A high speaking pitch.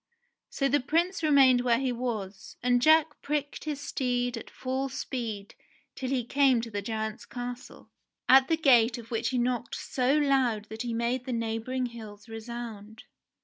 Yes: high, 245 Hz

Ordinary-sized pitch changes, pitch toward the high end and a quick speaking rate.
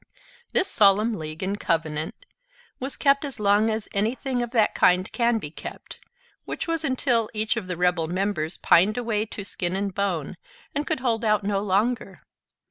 No: average, 4.4 semitones; high, 210 Hz; average, 175 wpm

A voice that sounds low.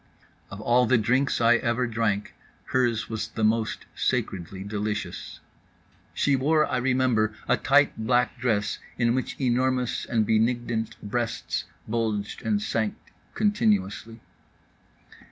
Yes: low, 115 Hz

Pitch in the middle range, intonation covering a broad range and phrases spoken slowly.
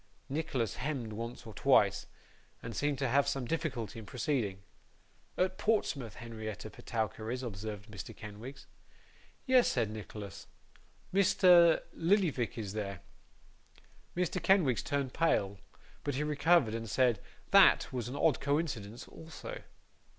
No: low, 125 Hz; wide, 6.0 semitones; slow, 130 wpm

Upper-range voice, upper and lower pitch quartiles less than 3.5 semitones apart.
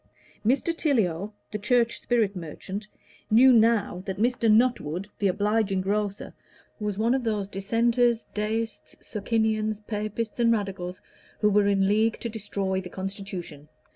Yes: high, 210 Hz; average, 2.7 semitones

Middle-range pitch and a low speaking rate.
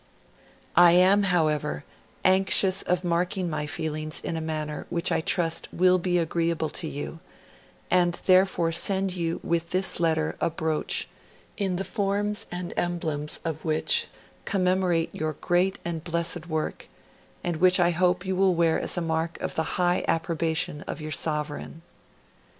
No: medium, 170 Hz; average, 150 wpm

